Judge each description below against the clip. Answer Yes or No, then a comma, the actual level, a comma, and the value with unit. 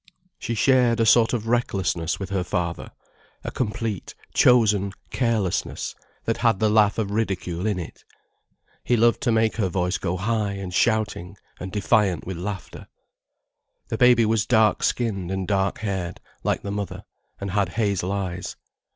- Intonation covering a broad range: No, average, 3.2 semitones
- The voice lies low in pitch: Yes, low, 100 Hz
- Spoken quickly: No, average, 160 wpm